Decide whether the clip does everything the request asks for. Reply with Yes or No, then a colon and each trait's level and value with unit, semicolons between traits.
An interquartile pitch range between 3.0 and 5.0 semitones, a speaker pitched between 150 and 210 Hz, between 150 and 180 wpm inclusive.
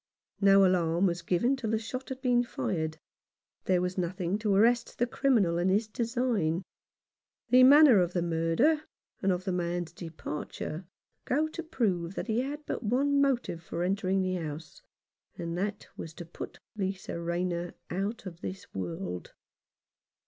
No: wide, 5.6 semitones; high, 190 Hz; average, 160 wpm